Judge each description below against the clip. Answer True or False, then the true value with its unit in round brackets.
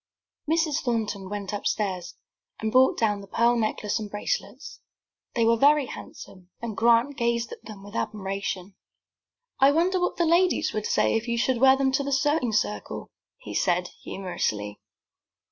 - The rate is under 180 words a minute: True (160 wpm)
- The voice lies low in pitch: False (230 Hz)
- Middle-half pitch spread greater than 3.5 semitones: True (5.1 semitones)